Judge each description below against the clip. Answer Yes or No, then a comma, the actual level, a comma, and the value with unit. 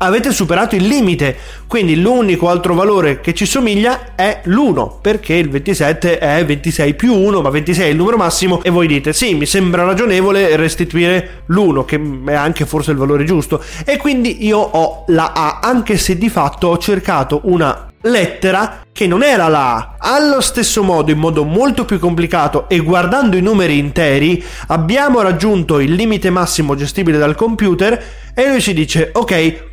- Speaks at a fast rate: Yes, fast, 175 wpm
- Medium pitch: Yes, medium, 180 Hz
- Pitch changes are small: No, average, 4.8 semitones